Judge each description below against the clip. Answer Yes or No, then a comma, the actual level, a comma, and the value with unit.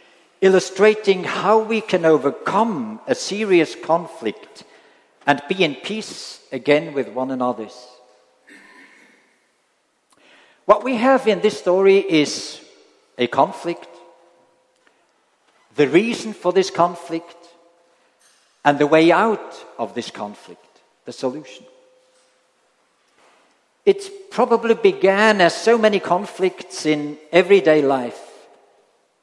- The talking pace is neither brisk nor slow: No, slow, 100 wpm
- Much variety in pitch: Yes, wide, 5.7 semitones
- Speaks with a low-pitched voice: No, medium, 180 Hz